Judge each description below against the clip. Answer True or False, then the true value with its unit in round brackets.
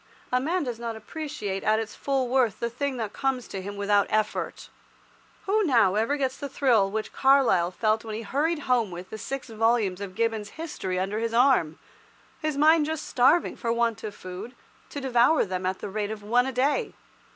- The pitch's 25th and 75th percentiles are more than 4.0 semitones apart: True (4.7 semitones)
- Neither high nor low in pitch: False (230 Hz)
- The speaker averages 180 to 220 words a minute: True (200 wpm)